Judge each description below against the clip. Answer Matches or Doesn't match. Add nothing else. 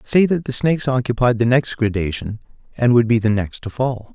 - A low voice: Matches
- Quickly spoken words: Matches